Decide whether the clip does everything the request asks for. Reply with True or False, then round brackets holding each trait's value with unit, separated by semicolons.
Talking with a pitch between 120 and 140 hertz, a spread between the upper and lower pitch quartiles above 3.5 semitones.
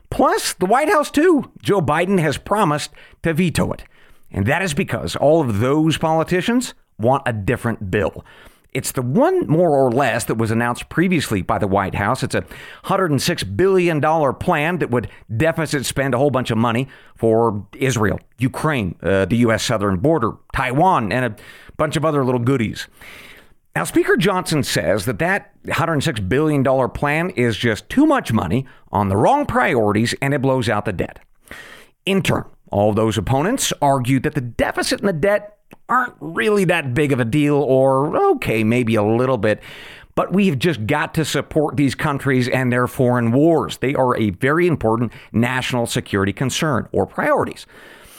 True (135 Hz; 5.6 semitones)